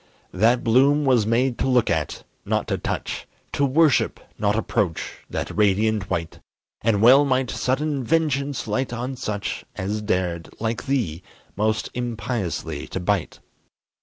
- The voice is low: Yes, low, 115 Hz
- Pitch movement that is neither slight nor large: Yes, average, 4.4 semitones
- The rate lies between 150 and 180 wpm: No, average, 140 wpm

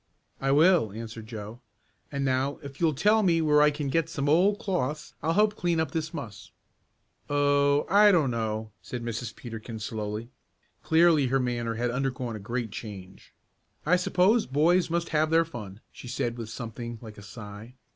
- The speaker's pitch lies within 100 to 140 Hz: Yes, low, 135 Hz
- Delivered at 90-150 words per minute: No, average, 175 wpm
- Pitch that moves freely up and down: Yes, wide, 6.0 semitones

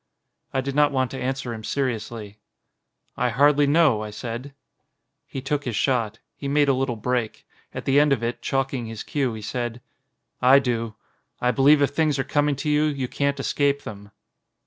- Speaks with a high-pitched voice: No, low, 135 Hz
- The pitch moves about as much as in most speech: Yes, average, 3.3 semitones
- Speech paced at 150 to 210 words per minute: Yes, average, 190 wpm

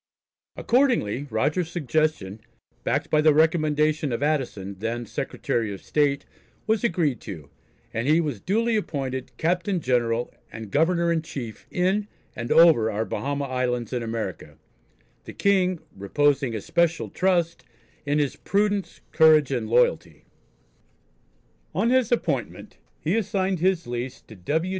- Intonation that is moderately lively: No, wide, 6.4 semitones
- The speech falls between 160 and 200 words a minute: No, slow, 135 wpm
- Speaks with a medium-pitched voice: Yes, medium, 150 Hz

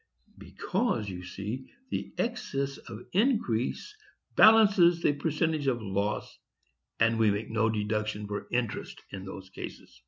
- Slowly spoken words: Yes, slow, 130 wpm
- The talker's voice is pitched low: Yes, low, 115 Hz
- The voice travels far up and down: Yes, wide, 7.6 semitones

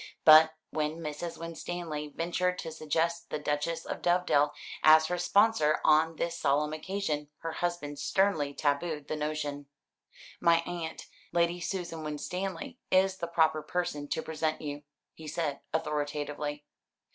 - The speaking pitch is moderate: Yes, medium, 160 Hz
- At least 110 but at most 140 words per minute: Yes, slow, 135 wpm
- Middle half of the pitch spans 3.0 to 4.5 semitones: No, narrow, 2.5 semitones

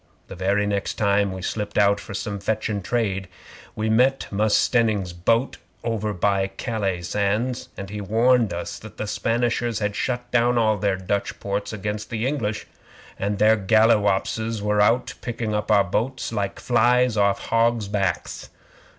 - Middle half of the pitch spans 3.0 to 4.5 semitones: No, narrow, 2.4 semitones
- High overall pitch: No, low, 105 Hz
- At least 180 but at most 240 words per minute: No, average, 160 wpm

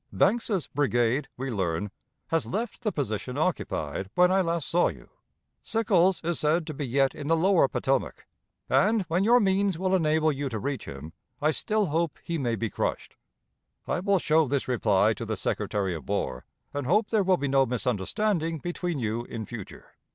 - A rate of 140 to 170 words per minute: No, average, 185 wpm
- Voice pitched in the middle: Yes, medium, 155 Hz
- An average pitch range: No, wide, 7.3 semitones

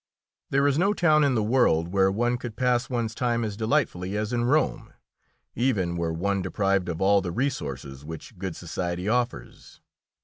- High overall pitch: No, low, 105 Hz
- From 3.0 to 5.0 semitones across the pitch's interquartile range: No, wide, 5.6 semitones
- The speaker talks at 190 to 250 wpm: No, average, 175 wpm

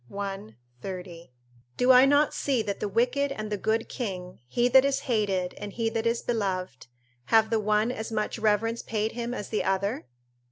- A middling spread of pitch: Yes, average, 3.3 semitones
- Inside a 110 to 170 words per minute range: No, average, 190 wpm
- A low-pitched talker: No, high, 220 Hz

